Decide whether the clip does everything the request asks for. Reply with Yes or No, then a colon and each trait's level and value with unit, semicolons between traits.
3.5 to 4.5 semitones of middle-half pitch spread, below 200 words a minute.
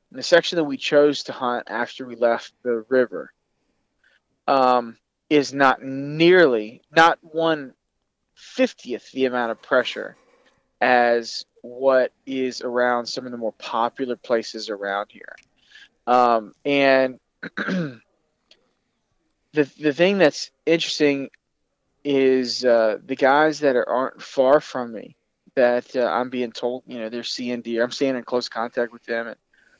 No: average, 2.9 semitones; average, 140 wpm